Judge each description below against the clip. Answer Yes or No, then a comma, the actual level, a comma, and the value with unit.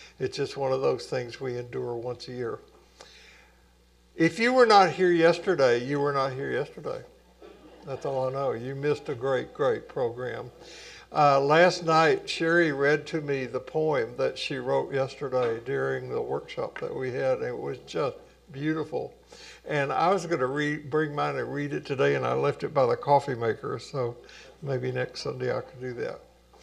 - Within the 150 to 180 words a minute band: No, average, 190 wpm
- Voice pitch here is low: No, medium, 145 Hz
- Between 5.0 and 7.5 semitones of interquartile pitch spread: Yes, wide, 5.6 semitones